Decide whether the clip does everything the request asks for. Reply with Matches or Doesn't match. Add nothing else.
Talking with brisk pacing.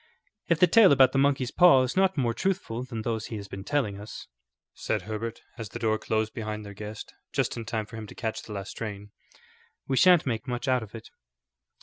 Matches